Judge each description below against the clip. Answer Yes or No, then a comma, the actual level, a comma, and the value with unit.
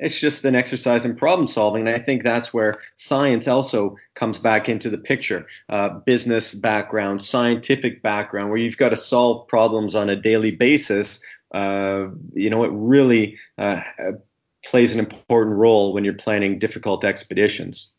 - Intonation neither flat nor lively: No, narrow, 2.3 semitones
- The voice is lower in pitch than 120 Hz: Yes, low, 110 Hz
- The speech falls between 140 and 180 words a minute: Yes, average, 165 wpm